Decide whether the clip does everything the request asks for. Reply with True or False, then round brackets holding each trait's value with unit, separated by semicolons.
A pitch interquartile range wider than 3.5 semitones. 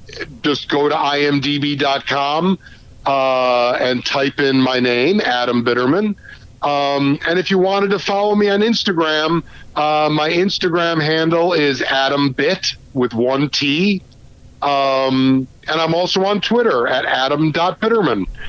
True (4.7 semitones)